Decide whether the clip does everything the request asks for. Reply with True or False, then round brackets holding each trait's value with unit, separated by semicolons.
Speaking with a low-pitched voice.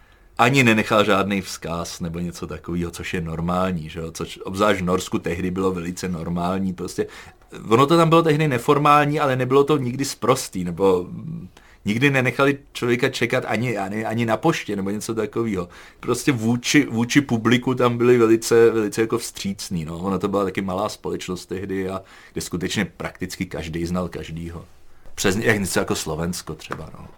True (100 Hz)